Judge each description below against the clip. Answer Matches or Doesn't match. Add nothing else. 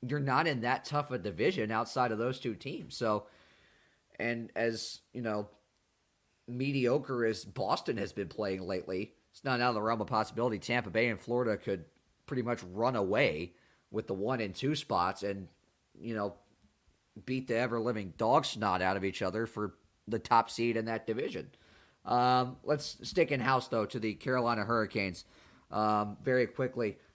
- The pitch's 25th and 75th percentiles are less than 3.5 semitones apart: Matches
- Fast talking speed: Doesn't match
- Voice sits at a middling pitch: Doesn't match